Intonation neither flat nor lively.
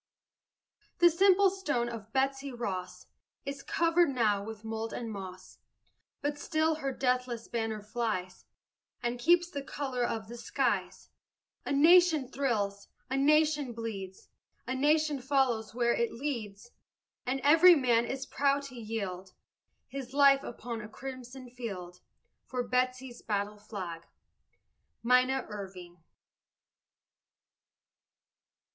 Yes: average, 4.3 semitones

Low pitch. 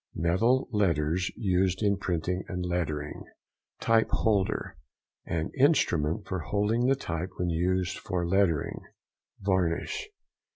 Yes: very low, 90 Hz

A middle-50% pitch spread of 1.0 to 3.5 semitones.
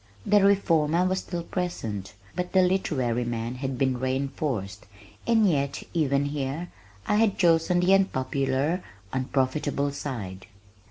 No: wide, 5.5 semitones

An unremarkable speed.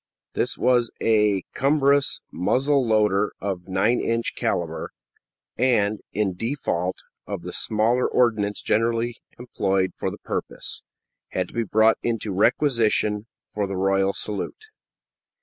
No: slow, 125 wpm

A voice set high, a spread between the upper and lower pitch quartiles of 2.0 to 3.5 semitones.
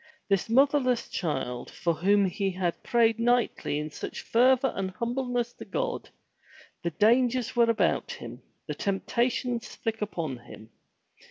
No: high, 230 Hz; average, 4.8 semitones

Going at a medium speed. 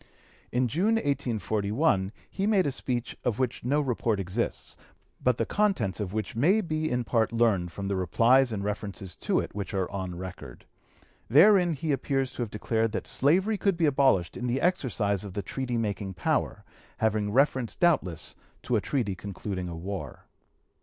Yes: average, 175 wpm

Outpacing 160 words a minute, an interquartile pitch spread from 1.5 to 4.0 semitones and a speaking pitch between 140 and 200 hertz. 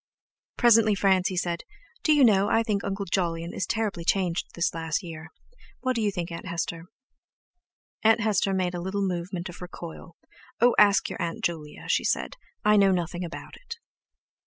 Yes: average, 175 wpm; average, 3.5 semitones; medium, 185 Hz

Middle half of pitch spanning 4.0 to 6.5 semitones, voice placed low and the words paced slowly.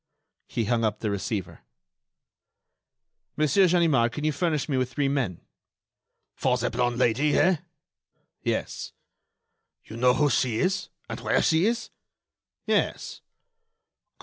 Yes: average, 4.7 semitones; low, 130 Hz; slow, 125 wpm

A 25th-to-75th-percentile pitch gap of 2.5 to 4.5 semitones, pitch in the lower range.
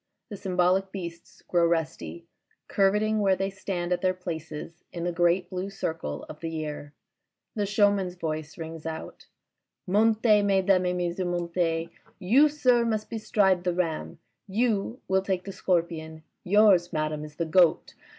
No: average, 3.1 semitones; medium, 180 Hz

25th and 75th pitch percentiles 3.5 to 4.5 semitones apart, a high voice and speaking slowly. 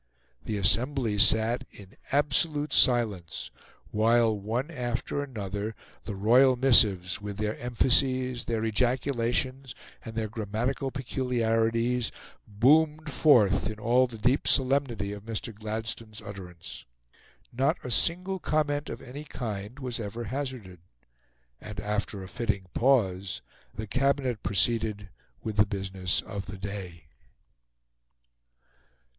No: average, 4.0 semitones; low, 115 Hz; slow, 115 wpm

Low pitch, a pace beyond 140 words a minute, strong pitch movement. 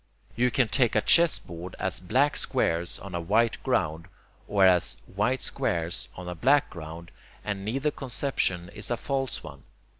Yes: low, 100 Hz; average, 160 wpm; wide, 6.8 semitones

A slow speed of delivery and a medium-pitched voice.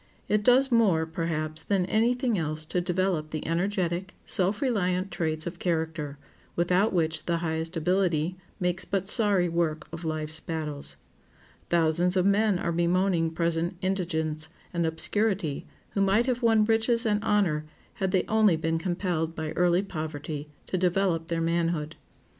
No: average, 155 wpm; medium, 175 Hz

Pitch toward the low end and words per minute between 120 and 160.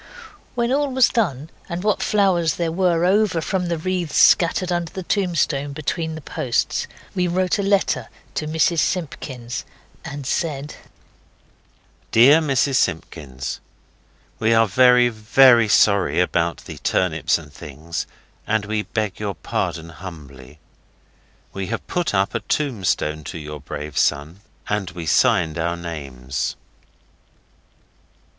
Yes: low, 125 Hz; slow, 135 wpm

